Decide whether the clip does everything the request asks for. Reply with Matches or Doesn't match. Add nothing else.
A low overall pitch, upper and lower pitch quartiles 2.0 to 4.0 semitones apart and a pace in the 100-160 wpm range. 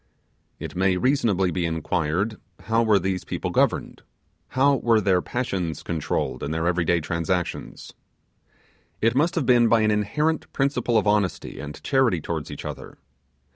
Doesn't match